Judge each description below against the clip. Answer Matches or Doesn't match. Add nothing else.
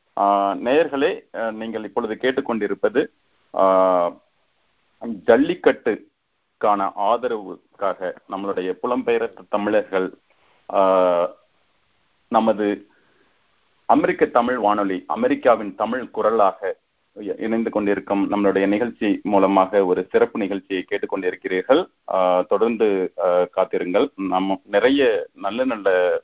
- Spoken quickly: Doesn't match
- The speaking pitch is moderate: Doesn't match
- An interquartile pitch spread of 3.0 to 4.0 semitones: Doesn't match